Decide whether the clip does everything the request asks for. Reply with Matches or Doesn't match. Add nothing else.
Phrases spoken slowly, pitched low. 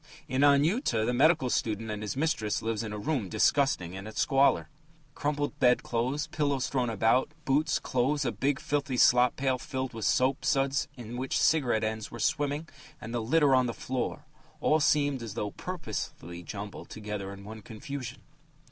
Doesn't match